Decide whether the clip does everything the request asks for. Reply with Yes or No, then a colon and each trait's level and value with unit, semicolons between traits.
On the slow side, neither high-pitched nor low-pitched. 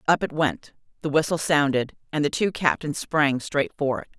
No: average, 200 wpm; medium, 145 Hz